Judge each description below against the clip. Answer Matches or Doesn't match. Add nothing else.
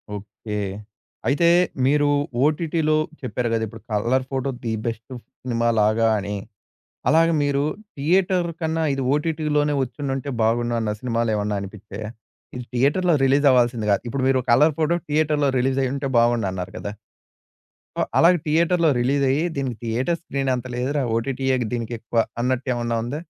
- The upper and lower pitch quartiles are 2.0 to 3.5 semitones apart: Doesn't match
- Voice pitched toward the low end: Matches